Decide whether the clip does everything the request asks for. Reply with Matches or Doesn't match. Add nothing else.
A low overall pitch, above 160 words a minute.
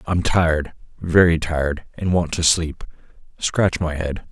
Doesn't match